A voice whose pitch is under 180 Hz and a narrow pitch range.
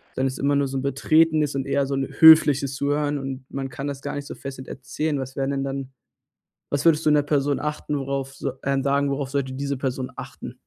Yes: medium, 140 Hz; narrow, 1.2 semitones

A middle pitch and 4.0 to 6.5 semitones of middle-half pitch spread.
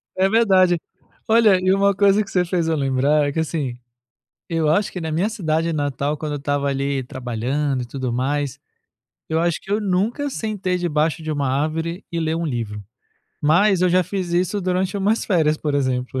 Yes: medium, 160 Hz; average, 4.6 semitones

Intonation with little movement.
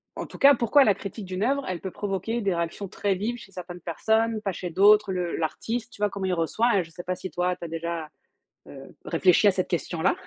No: average, 3.4 semitones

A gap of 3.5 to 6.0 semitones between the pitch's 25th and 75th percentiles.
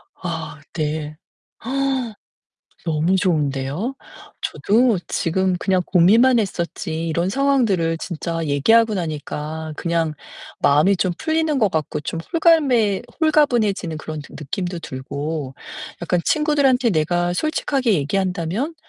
No: wide, 6.6 semitones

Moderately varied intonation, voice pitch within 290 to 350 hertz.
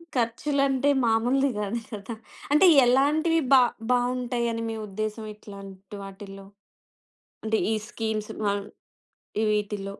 No: average, 3.6 semitones; high, 225 Hz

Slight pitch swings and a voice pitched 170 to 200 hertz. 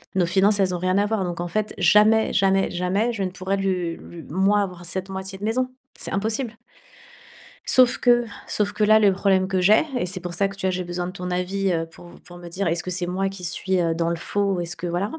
Yes: narrow, 2.3 semitones; high, 190 Hz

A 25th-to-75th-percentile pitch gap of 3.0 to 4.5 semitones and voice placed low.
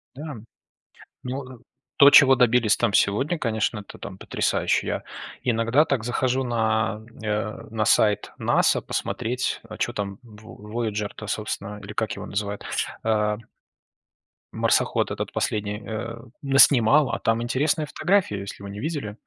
Yes: average, 3.5 semitones; low, 115 Hz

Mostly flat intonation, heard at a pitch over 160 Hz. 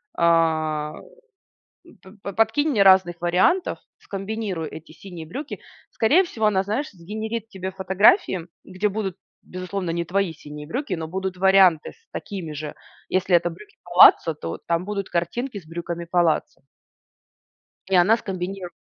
No: average, 3.7 semitones; medium, 185 Hz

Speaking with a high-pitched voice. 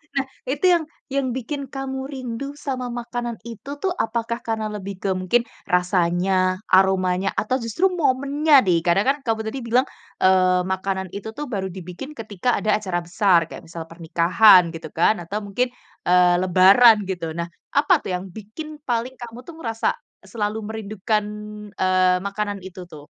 Yes: high, 210 Hz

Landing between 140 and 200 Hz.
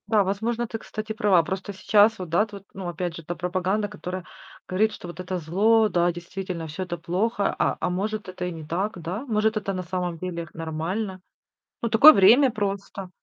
Yes: high, 190 Hz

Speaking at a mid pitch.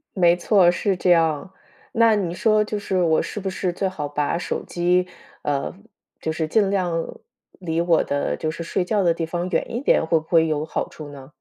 Yes: medium, 175 Hz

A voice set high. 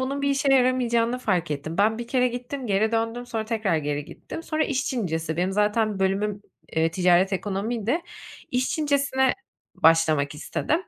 Yes: high, 220 Hz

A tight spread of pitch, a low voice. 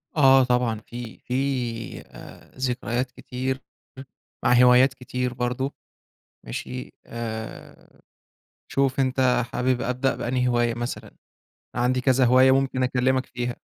Yes: narrow, 1.1 semitones; low, 125 Hz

